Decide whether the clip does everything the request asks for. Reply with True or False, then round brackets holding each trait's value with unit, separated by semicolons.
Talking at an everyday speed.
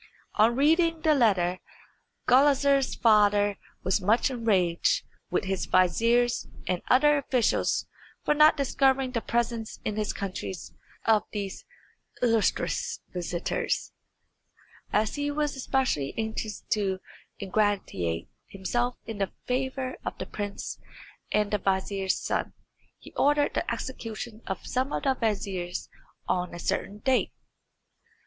False (125 wpm)